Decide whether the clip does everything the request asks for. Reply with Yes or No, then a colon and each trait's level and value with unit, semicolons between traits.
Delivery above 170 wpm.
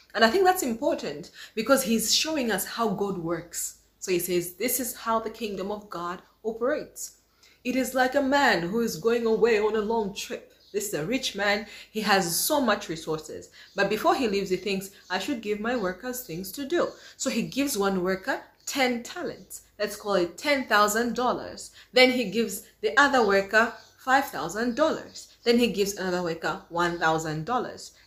Yes: average, 180 wpm